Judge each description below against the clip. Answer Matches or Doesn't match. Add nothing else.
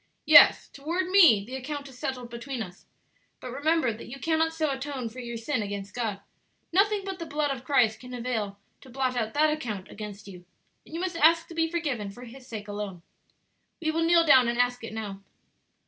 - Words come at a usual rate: Doesn't match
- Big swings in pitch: Matches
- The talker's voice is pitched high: Matches